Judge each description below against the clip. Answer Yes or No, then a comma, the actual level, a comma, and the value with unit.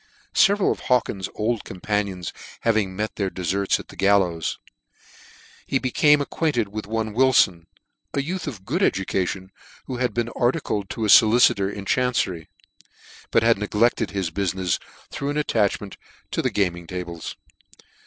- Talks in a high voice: No, low, 105 Hz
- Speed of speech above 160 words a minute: No, average, 155 wpm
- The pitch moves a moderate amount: Yes, average, 4.3 semitones